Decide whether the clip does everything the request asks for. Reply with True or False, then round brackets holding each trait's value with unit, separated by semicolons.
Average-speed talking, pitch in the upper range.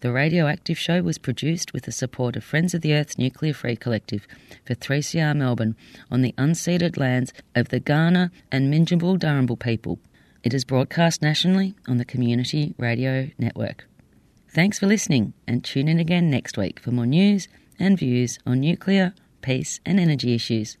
False (175 wpm; 135 Hz)